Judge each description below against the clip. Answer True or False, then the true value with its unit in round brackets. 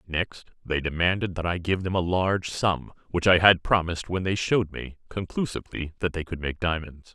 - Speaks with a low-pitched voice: True (90 Hz)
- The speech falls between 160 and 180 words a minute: False (200 wpm)